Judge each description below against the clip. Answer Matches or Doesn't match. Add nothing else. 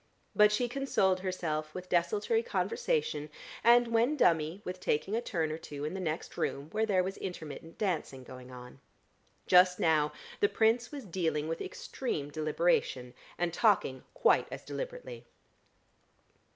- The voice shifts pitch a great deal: Matches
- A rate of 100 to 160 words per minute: Matches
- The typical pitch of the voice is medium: Matches